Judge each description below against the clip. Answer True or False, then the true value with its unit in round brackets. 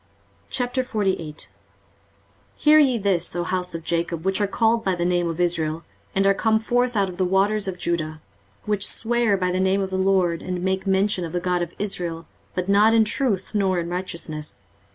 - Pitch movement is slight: False (3.1 semitones)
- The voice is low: False (190 Hz)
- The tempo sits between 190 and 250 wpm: True (195 wpm)